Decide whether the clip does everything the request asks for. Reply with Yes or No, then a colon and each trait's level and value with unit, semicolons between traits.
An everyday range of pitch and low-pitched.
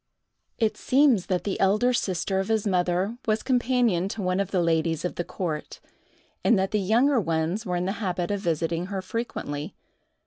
No: average, 3.9 semitones; high, 190 Hz